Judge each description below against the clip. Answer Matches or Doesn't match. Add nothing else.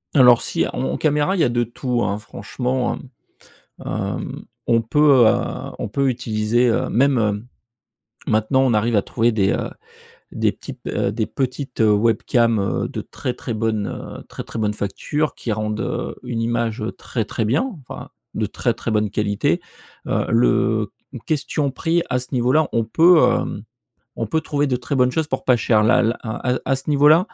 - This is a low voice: Matches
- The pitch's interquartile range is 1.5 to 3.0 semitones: Doesn't match